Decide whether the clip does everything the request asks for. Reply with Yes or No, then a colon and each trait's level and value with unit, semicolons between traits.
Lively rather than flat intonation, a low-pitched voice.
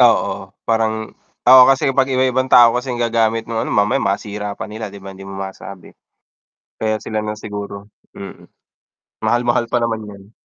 No: average, 2.8 semitones; low, 110 Hz